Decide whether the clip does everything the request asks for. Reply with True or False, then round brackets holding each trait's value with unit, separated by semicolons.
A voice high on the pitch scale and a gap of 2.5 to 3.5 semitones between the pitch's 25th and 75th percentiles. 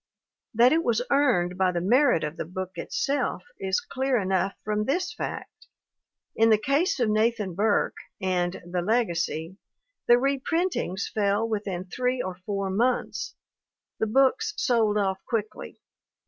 False (215 Hz; 5.2 semitones)